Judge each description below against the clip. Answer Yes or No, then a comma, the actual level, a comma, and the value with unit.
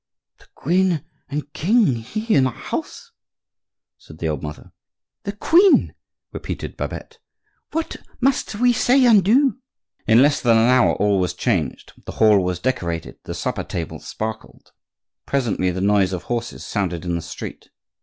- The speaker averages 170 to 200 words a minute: No, average, 155 wpm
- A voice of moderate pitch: No, low, 120 Hz